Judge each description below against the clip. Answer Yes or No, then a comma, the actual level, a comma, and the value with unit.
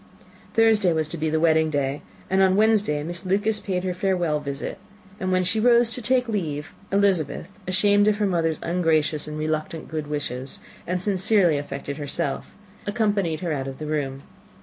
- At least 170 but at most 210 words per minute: Yes, average, 175 wpm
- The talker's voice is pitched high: No, medium, 170 Hz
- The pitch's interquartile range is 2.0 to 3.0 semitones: No, average, 4.9 semitones